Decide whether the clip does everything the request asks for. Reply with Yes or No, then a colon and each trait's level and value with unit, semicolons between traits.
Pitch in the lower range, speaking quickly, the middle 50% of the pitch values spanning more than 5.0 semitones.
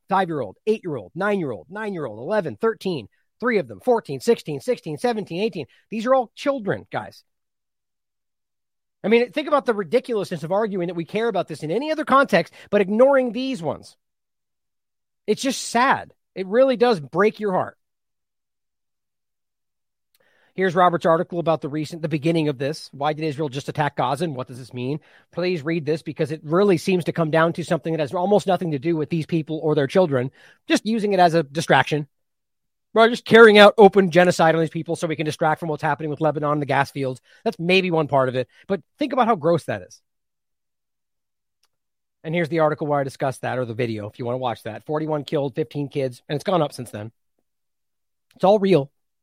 No: medium, 165 Hz; fast, 210 wpm; wide, 5.4 semitones